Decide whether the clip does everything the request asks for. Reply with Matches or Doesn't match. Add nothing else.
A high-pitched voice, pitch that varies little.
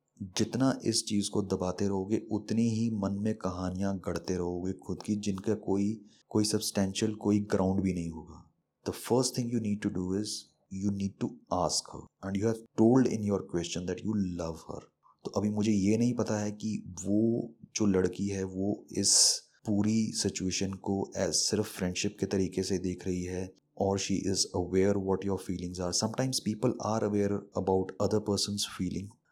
Doesn't match